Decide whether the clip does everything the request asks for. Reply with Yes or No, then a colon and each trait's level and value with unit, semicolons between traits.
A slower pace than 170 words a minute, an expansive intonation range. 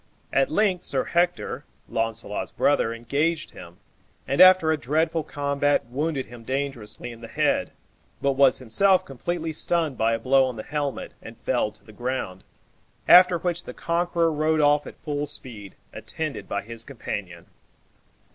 Yes: average, 155 wpm; wide, 5.7 semitones